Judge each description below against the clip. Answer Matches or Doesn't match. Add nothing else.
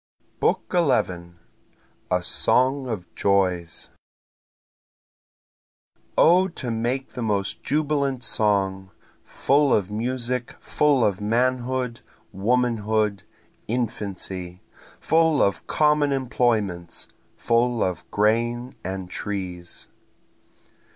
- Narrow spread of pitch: Doesn't match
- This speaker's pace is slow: Matches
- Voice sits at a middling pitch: Doesn't match